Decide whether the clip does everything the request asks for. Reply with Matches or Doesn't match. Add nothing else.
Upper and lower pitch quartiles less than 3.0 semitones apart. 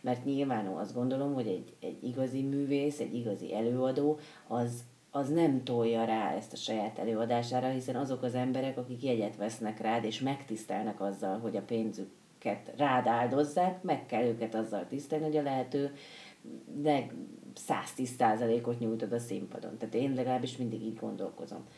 Doesn't match